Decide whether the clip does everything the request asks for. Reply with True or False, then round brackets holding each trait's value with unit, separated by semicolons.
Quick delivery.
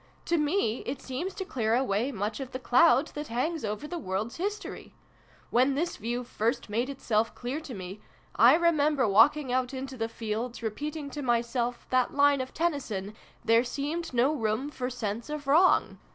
False (190 wpm)